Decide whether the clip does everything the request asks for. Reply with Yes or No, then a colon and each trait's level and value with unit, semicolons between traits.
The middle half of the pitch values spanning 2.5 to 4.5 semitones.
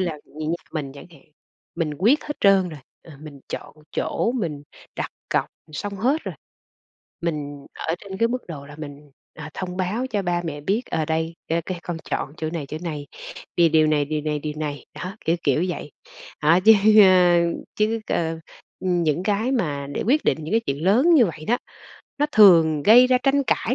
No: average, 5.1 semitones